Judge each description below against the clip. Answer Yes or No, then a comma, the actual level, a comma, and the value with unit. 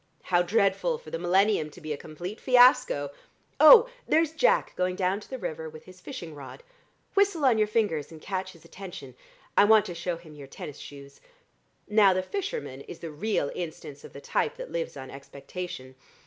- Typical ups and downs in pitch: No, wide, 6.6 semitones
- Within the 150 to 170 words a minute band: No, average, 190 wpm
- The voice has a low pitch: No, medium, 185 Hz